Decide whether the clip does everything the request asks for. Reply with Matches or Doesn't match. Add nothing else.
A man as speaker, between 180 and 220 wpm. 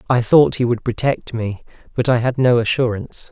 Matches